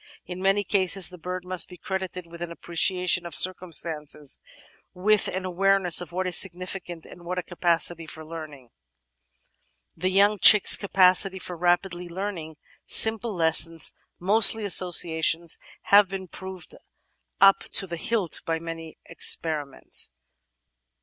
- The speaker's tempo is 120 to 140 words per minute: Yes, slow, 135 wpm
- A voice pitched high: No, medium, 180 Hz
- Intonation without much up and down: Yes, narrow, 2.3 semitones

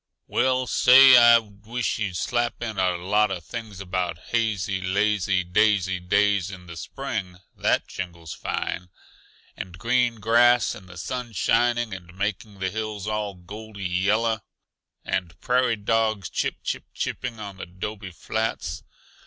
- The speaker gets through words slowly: No, average, 145 wpm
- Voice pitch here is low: Yes, low, 105 Hz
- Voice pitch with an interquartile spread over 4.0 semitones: No, average, 3.7 semitones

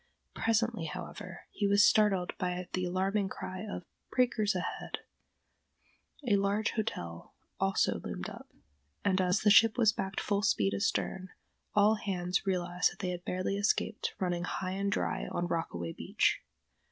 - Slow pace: No, average, 150 wpm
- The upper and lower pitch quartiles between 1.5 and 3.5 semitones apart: Yes, narrow, 2.5 semitones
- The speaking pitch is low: No, high, 190 Hz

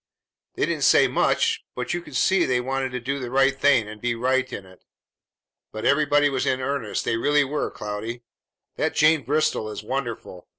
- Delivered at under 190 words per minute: No, average, 195 wpm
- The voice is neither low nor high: No, low, 130 Hz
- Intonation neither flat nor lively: Yes, average, 3.8 semitones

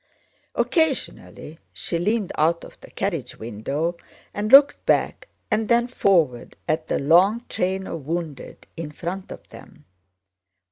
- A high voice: No, medium, 175 Hz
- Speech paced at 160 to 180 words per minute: No, slow, 135 wpm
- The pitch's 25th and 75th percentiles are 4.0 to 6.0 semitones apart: Yes, average, 5.2 semitones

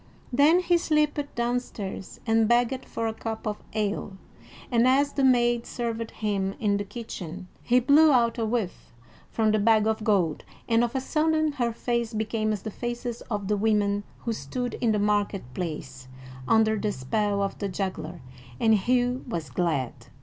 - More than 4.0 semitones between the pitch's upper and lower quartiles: No, average, 3.2 semitones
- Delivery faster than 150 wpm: Yes, average, 175 wpm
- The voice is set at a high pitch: Yes, high, 220 Hz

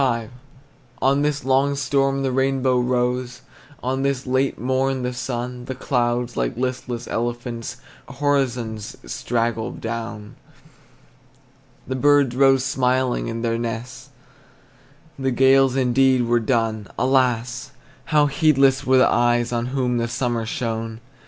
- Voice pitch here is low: Yes, low, 125 Hz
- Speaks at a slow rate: Yes, slow, 125 wpm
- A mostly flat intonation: Yes, narrow, 2.1 semitones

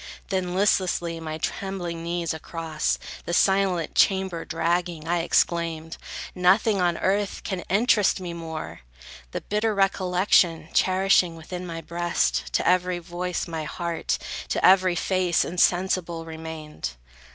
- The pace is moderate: No, slow, 125 wpm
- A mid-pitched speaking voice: Yes, medium, 175 Hz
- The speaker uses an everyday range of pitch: No, narrow, 2.2 semitones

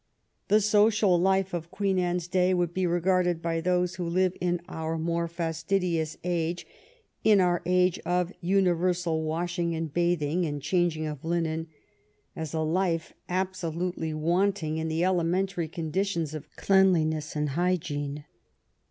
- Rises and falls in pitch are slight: Yes, narrow, 2.2 semitones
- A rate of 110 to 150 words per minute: Yes, average, 140 wpm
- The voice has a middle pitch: Yes, medium, 175 Hz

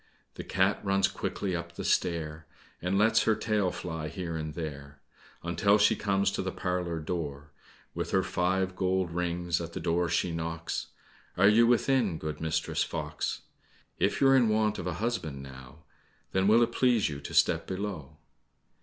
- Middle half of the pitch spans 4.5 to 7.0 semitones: No, average, 3.7 semitones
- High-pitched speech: No, very low, 90 Hz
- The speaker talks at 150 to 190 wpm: Yes, average, 170 wpm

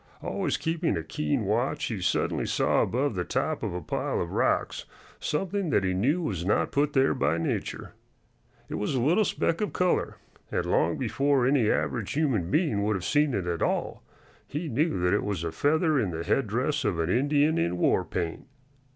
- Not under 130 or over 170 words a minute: No, average, 195 wpm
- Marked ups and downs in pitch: Yes, wide, 8.8 semitones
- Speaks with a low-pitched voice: Yes, low, 125 Hz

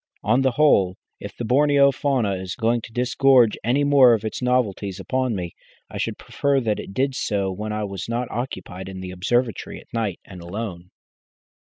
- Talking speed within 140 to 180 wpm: No, average, 190 wpm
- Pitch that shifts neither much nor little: Yes, average, 4.9 semitones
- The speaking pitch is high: No, low, 115 Hz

